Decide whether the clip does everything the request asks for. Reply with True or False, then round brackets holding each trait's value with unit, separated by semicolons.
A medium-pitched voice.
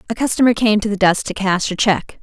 False (205 Hz)